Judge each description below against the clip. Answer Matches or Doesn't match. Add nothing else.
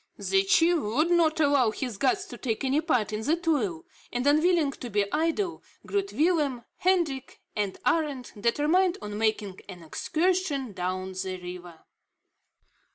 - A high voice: Matches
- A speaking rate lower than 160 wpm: Matches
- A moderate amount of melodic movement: Doesn't match